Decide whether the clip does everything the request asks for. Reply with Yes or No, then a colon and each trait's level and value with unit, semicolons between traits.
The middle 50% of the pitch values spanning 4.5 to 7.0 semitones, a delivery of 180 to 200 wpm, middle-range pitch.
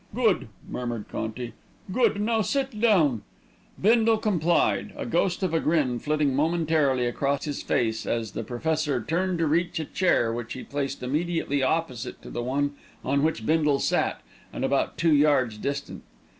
No: average, 5.2 semitones; average, 160 wpm; medium, 150 Hz